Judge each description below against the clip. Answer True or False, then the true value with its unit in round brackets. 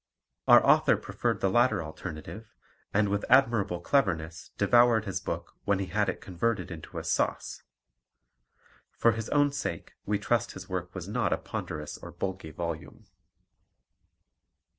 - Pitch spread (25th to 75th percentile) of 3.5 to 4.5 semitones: False (4.9 semitones)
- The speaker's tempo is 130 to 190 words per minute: True (145 wpm)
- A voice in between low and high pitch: False (100 Hz)